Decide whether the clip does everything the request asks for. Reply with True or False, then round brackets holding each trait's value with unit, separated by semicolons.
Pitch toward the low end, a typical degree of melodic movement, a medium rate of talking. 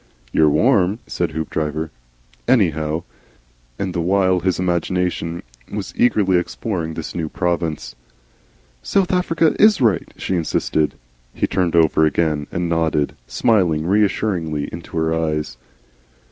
False (85 Hz; 3.3 semitones; 120 wpm)